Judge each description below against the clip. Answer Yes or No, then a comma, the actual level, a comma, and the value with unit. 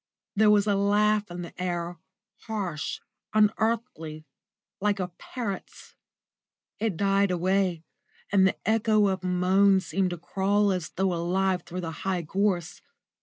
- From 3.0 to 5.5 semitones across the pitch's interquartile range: No, narrow, 2.5 semitones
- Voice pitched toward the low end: No, high, 190 Hz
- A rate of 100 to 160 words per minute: Yes, average, 140 wpm